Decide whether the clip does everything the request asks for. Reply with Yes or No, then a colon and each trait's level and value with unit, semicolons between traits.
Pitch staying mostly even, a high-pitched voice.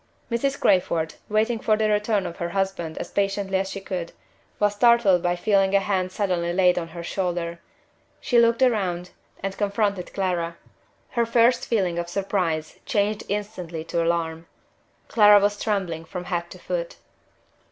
No: average, 3.3 semitones; high, 195 Hz